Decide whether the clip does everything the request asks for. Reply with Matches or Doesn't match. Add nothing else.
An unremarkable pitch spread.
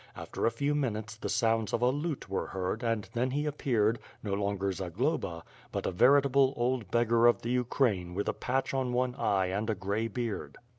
Matches